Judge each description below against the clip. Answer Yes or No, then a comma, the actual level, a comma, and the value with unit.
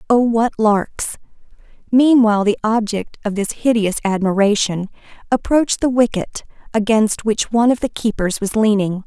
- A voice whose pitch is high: Yes, high, 220 Hz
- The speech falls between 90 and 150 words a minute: Yes, average, 140 wpm